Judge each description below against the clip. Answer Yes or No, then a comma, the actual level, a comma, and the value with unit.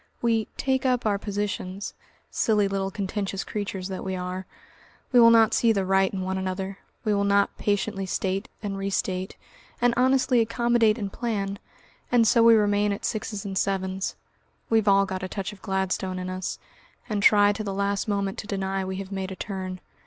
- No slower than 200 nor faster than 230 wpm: No, average, 185 wpm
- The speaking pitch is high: Yes, high, 200 Hz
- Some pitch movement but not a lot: No, narrow, 2.1 semitones